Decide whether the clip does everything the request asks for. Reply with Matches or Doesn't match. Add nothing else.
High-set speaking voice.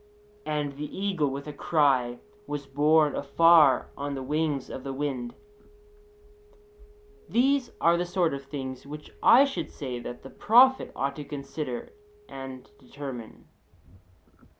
Doesn't match